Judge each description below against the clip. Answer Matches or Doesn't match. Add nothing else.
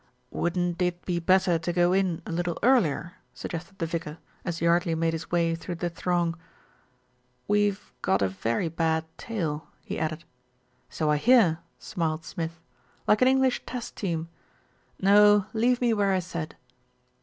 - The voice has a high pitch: Doesn't match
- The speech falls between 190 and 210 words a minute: Doesn't match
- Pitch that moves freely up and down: Doesn't match